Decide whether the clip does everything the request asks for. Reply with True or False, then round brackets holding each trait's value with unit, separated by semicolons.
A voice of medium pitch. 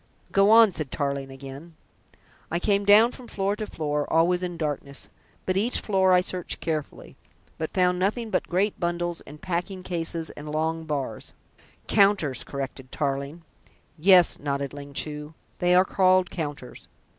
True (170 Hz)